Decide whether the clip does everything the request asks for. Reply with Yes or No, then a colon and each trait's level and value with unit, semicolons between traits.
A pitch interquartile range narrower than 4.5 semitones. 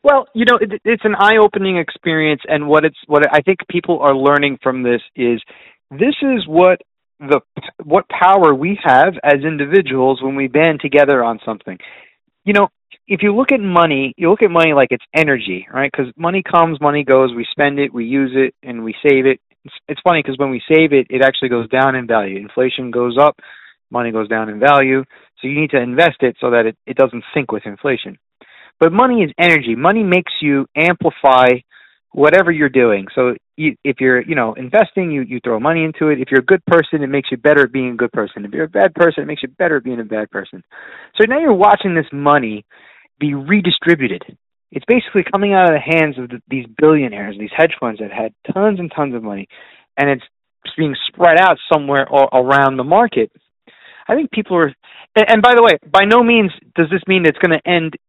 No: average, 5.3 semitones